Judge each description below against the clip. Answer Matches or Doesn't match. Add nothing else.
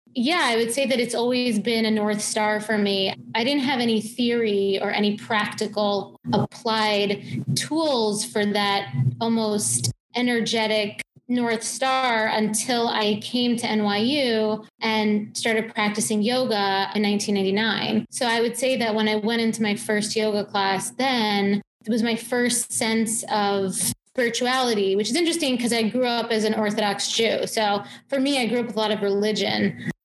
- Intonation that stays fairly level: Matches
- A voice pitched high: Matches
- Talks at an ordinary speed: Matches